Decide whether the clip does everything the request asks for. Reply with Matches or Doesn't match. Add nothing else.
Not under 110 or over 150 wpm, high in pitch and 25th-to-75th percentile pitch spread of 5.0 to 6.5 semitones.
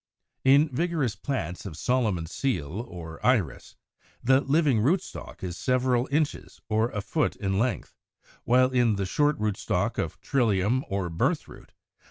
Doesn't match